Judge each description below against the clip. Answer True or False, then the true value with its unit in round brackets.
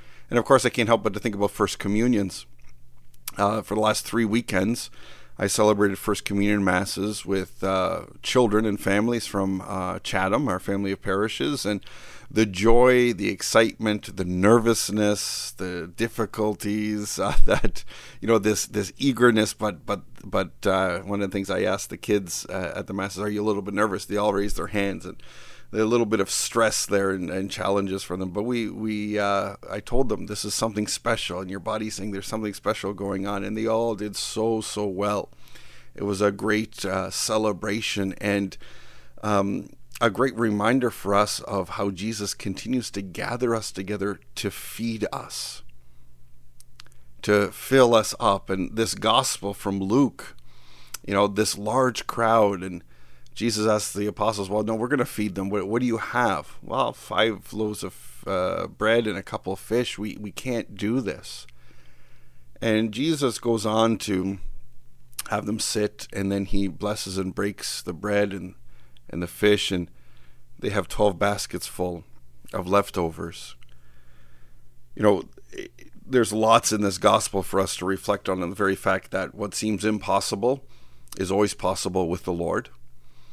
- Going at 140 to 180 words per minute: True (175 wpm)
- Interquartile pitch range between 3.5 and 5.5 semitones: False (2.6 semitones)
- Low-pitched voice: True (100 Hz)